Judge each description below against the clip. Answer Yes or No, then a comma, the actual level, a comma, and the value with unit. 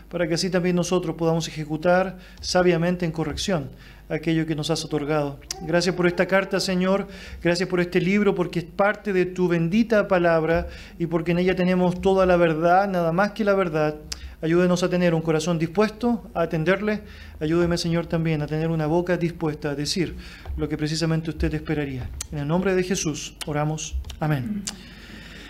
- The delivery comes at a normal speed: Yes, average, 175 wpm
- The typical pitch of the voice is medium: Yes, medium, 175 Hz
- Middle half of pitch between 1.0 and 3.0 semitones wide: Yes, narrow, 2.6 semitones